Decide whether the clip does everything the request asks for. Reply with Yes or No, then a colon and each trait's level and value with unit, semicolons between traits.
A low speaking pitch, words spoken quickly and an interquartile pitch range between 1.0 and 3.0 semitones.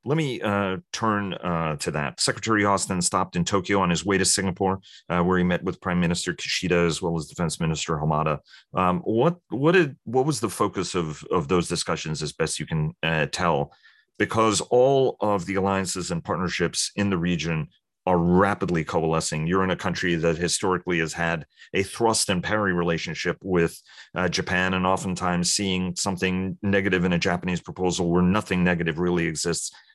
No: very low, 90 Hz; average, 185 wpm; narrow, 2.4 semitones